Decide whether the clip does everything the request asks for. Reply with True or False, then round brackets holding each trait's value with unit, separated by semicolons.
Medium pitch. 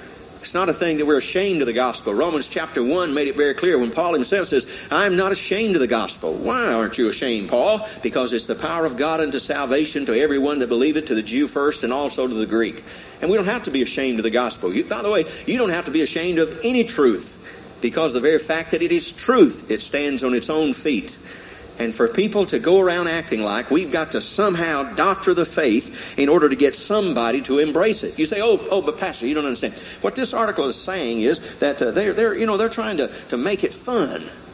True (155 Hz)